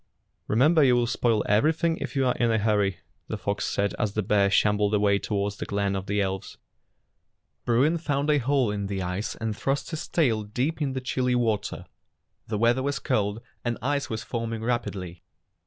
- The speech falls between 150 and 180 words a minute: No, average, 190 wpm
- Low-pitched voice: Yes, low, 115 Hz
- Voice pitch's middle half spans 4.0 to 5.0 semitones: Yes, average, 4.4 semitones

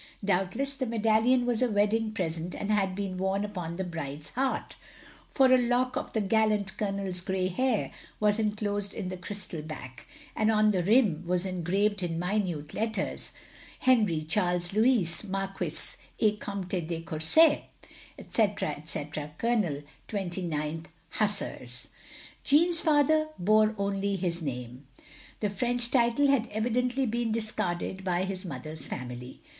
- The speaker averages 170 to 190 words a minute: No, average, 140 wpm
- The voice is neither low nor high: No, high, 200 Hz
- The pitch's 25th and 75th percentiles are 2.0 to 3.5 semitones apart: No, average, 4.3 semitones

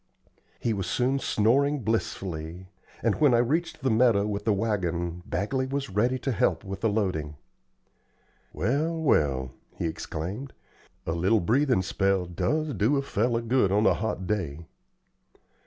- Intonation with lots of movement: Yes, wide, 5.7 semitones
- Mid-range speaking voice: No, low, 105 Hz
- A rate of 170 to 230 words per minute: No, average, 150 wpm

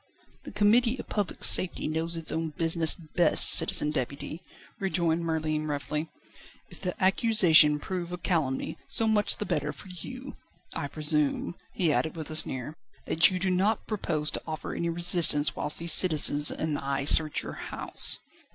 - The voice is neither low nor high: Yes, medium, 165 Hz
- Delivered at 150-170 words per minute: Yes, average, 165 wpm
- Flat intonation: No, average, 3.2 semitones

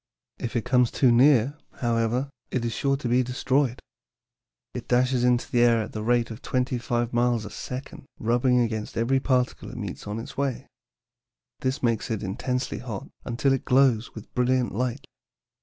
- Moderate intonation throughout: No, narrow, 1.8 semitones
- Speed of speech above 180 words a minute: No, average, 175 wpm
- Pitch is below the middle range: Yes, low, 125 Hz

